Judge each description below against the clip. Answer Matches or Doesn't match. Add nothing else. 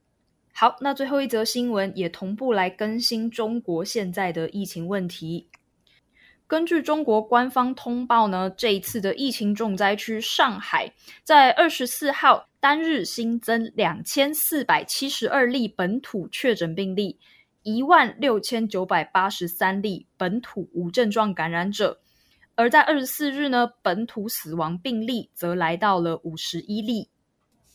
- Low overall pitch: Doesn't match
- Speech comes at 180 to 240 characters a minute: Matches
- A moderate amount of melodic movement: Matches